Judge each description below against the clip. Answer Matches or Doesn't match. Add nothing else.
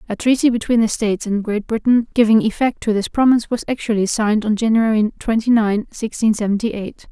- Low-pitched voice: Doesn't match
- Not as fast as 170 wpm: Doesn't match